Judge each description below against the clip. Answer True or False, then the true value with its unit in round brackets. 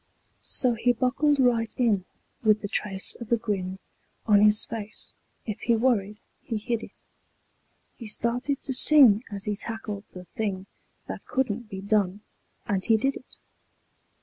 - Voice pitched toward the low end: False (220 Hz)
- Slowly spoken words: False (155 wpm)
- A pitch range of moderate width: True (3.0 semitones)